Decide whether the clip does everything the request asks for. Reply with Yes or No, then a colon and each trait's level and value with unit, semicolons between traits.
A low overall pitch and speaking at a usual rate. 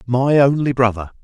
Yes: low, 125 Hz; average, 145 wpm